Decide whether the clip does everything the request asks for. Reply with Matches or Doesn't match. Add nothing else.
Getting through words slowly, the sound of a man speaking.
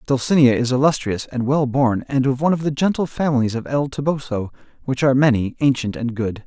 Doesn't match